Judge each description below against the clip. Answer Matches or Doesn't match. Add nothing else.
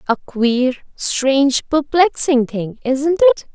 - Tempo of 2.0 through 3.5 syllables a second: Matches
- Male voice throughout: Doesn't match